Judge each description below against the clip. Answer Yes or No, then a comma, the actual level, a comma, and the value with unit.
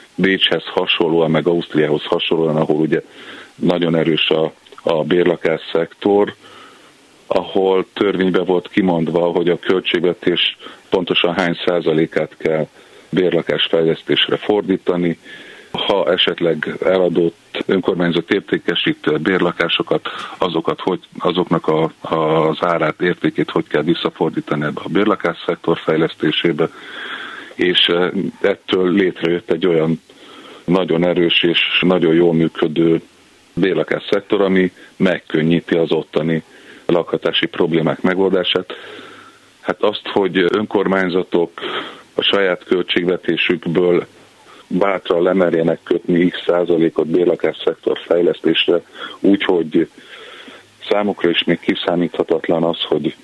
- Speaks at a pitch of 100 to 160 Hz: No, very low, 85 Hz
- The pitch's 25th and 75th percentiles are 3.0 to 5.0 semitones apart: No, narrow, 2.4 semitones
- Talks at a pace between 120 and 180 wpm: No, slow, 105 wpm